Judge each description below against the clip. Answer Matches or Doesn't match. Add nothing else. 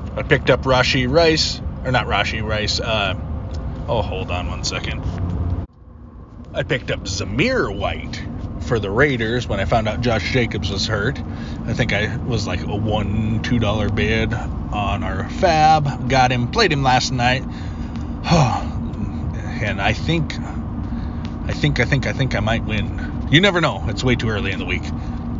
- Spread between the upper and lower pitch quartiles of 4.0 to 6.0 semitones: Matches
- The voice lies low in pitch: Matches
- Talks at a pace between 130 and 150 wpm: Doesn't match